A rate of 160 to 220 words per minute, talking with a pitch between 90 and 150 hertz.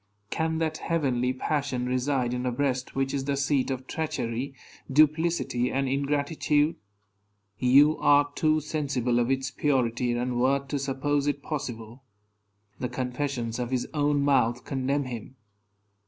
No: average, 140 wpm; low, 135 Hz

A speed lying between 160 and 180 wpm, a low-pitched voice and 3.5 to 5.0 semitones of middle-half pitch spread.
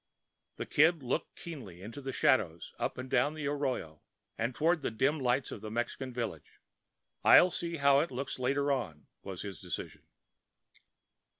Yes: average, 165 wpm; low, 130 Hz; average, 4.1 semitones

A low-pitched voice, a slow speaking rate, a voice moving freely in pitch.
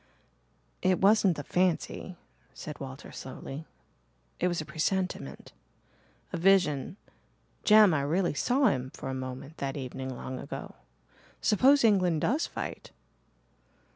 No: medium, 165 Hz; slow, 125 wpm; wide, 6.0 semitones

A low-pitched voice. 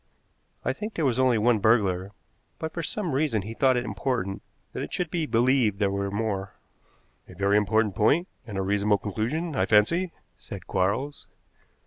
Yes: low, 110 Hz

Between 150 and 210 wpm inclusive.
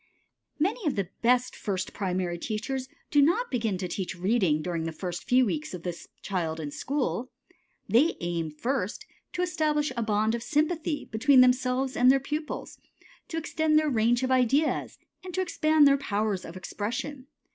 Yes: average, 170 wpm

